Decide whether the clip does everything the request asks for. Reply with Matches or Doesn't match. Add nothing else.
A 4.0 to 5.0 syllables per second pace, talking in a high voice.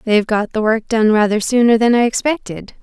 Doesn't match